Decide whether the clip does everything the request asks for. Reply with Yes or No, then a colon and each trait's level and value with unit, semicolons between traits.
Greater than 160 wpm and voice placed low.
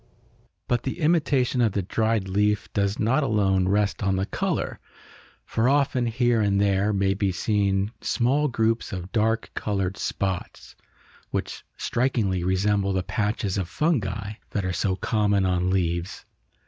No: average, 150 wpm; low, 100 Hz